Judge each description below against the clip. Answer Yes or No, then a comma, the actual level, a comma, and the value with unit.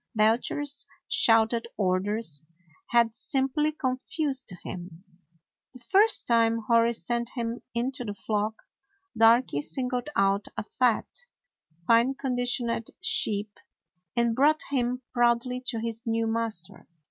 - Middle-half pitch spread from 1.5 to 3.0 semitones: Yes, narrow, 2.4 semitones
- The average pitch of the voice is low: No, high, 235 Hz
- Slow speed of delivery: Yes, slow, 110 wpm